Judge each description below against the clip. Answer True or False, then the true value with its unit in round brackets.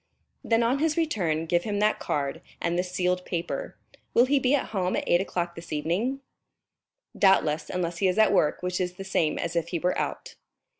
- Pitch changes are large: False (4.1 semitones)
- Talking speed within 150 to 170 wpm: False (205 wpm)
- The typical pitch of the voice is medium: True (180 Hz)